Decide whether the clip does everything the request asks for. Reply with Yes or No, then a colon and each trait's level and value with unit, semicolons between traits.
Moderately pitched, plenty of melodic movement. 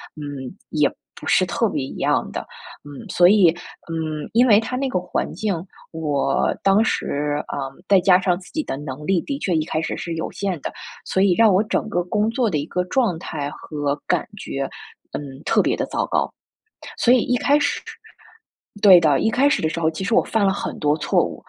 Yes: medium, 180 Hz; wide, 6.1 semitones